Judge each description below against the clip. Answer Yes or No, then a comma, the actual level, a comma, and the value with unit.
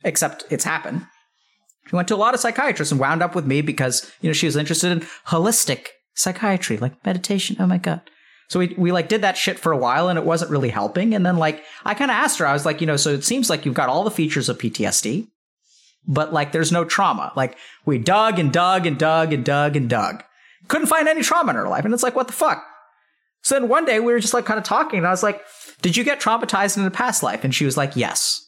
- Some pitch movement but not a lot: No, wide, 6.5 semitones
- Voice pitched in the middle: Yes, medium, 180 Hz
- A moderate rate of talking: No, fast, 265 wpm